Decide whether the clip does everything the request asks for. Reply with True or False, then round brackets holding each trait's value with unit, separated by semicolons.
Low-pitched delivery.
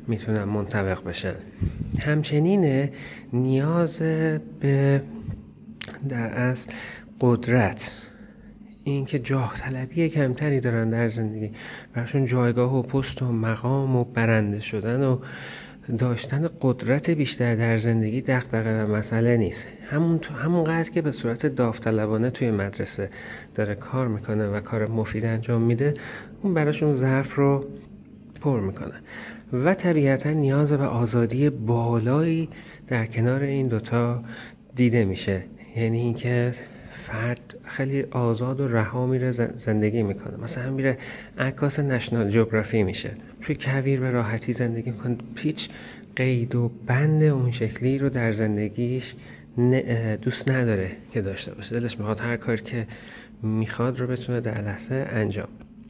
True (120 Hz)